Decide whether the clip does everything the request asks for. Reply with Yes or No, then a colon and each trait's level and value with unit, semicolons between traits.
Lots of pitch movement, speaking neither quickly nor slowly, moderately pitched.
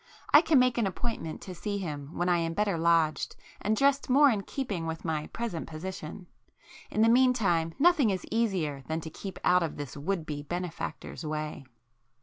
Yes: wide, 5.8 semitones; average, 180 wpm; medium, 180 Hz